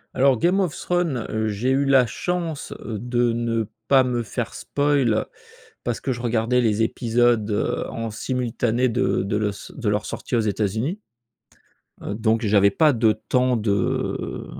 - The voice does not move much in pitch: No, average, 3.0 semitones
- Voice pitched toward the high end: No, low, 120 Hz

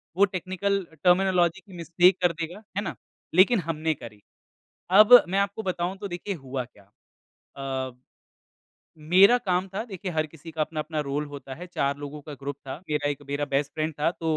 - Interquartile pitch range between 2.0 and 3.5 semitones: No, average, 4.3 semitones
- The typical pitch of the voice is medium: Yes, medium, 165 Hz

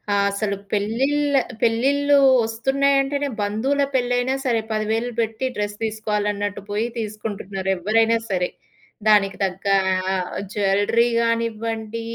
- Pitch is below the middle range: No, high, 220 Hz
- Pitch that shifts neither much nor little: Yes, average, 3.2 semitones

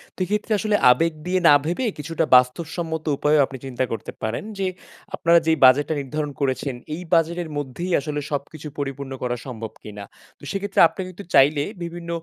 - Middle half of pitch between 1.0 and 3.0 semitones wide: No, average, 4.1 semitones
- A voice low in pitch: No, medium, 155 Hz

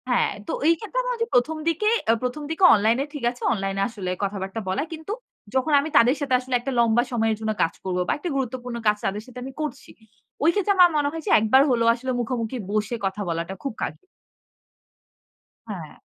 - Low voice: No, high, 245 Hz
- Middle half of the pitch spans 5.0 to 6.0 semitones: Yes, average, 5.3 semitones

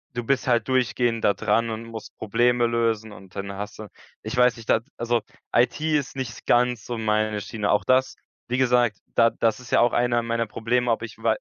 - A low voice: Yes, low, 115 Hz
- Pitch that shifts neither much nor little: No, narrow, 2.0 semitones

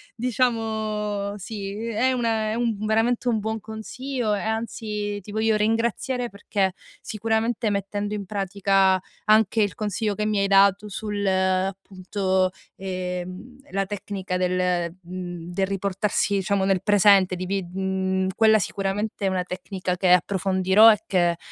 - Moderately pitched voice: No, high, 200 Hz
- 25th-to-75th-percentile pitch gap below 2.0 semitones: No, narrow, 2.5 semitones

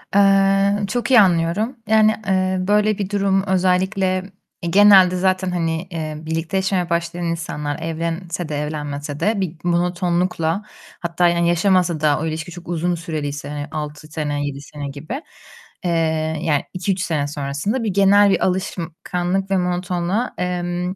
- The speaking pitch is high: No, medium, 175 Hz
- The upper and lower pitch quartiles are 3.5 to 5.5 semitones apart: No, average, 3.0 semitones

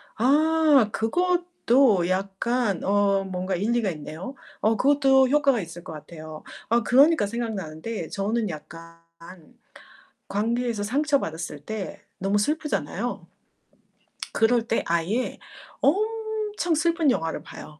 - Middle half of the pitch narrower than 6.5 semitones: No, wide, 7.0 semitones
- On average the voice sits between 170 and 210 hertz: No, high, 225 Hz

